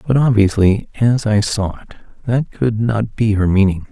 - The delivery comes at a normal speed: Yes, average, 185 wpm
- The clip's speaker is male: Yes, male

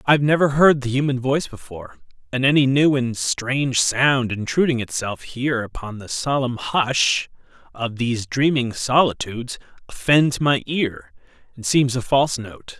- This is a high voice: No, low, 130 Hz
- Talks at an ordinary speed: Yes, average, 155 wpm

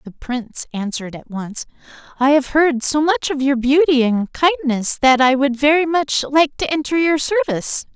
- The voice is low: No, very high, 280 Hz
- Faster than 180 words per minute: Yes, average, 190 wpm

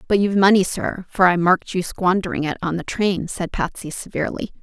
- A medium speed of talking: No, fast, 210 wpm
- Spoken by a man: No, female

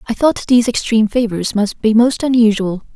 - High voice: Yes, high, 225 Hz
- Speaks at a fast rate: No, average, 185 wpm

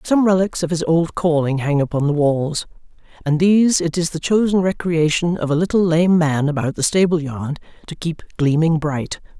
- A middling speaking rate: Yes, average, 190 wpm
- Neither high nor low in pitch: Yes, medium, 165 Hz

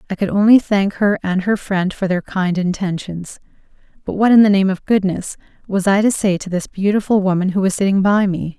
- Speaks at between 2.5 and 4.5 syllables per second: No, 5.4 syllables/s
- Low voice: No, high, 195 Hz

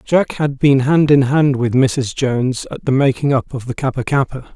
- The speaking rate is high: Yes, fast, 225 wpm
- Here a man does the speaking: Yes, male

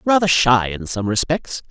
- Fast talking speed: No, average, 175 wpm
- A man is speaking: Yes, male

